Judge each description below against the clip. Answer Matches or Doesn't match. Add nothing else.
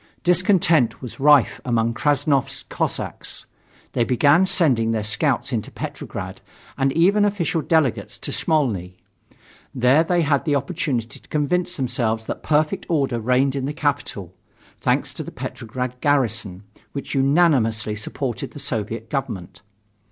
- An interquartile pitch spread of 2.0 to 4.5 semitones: Doesn't match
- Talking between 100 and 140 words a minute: Matches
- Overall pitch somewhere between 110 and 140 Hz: Matches